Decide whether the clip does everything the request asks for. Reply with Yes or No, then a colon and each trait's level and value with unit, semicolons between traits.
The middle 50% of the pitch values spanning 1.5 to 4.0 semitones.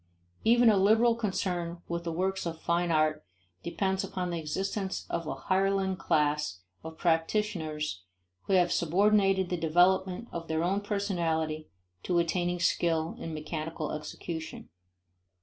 Yes: average, 3.1 semitones